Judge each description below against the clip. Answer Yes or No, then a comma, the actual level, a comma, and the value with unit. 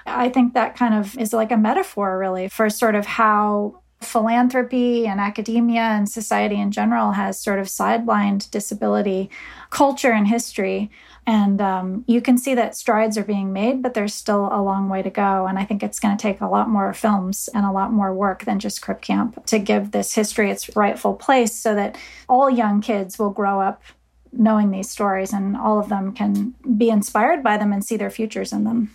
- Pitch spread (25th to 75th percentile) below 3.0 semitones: Yes, narrow, 2.5 semitones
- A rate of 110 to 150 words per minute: No, fast, 205 wpm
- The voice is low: No, high, 210 Hz